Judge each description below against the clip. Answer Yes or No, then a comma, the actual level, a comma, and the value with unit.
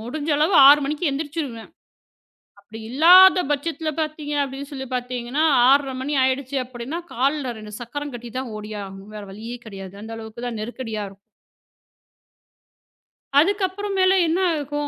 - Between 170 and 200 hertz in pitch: No, very high, 265 Hz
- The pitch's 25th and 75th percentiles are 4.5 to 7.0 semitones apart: Yes, average, 4.8 semitones